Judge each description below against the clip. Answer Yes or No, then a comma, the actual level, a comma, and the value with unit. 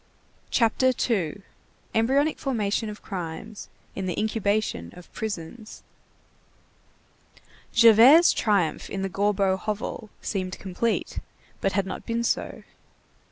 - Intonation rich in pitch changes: No, average, 3.2 semitones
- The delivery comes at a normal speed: No, slow, 105 wpm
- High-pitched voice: Yes, high, 210 Hz